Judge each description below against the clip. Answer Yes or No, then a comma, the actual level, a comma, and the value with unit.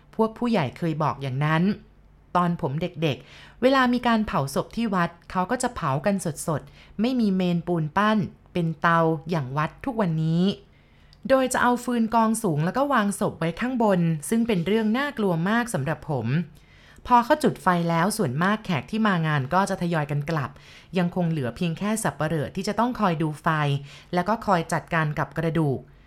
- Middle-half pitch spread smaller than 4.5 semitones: No, average, 5.3 semitones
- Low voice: No, medium, 175 Hz